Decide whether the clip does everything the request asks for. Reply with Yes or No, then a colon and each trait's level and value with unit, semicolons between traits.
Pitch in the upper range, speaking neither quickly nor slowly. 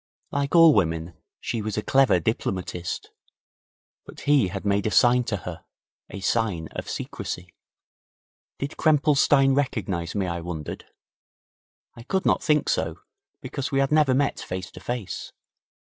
No: low, 110 Hz; average, 150 wpm